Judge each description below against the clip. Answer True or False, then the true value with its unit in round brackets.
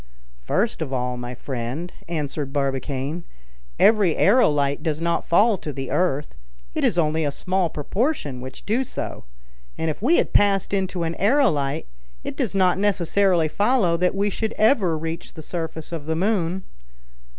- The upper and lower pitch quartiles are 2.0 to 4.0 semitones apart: False (5.2 semitones)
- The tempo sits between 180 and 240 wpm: False (160 wpm)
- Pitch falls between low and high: True (170 Hz)